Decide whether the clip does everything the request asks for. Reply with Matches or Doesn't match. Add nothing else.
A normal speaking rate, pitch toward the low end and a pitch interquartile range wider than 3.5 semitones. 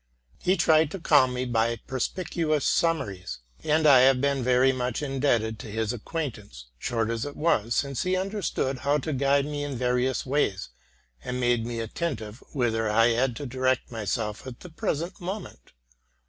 Matches